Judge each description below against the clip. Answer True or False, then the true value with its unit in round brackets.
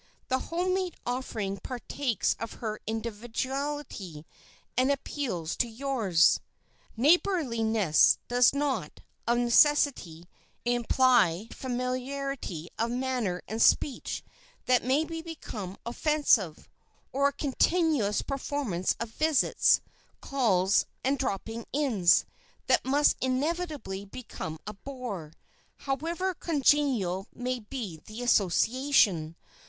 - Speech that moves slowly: True (100 wpm)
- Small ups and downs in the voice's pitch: False (5.3 semitones)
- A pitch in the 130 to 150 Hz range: False (245 Hz)